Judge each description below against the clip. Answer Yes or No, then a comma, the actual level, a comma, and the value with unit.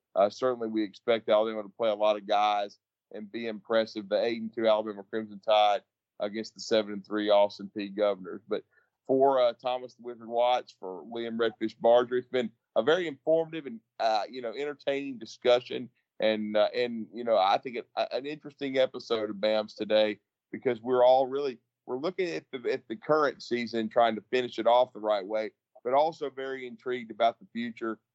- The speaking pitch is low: Yes, low, 115 Hz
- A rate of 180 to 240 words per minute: Yes, average, 200 wpm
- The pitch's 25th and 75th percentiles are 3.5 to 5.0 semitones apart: No, average, 2.8 semitones